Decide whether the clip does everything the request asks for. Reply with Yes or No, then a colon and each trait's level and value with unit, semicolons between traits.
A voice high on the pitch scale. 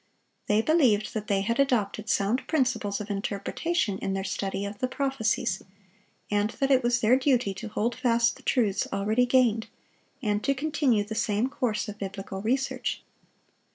Yes: high, 220 Hz